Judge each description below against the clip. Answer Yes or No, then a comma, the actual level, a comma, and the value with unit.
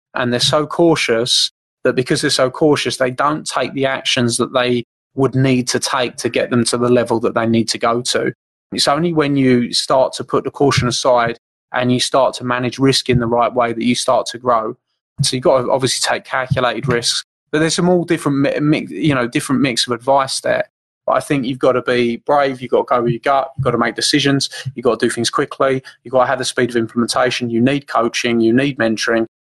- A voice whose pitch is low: Yes, low, 125 Hz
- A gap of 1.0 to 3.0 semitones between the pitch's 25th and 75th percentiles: Yes, average, 2.7 semitones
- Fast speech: Yes, fast, 240 wpm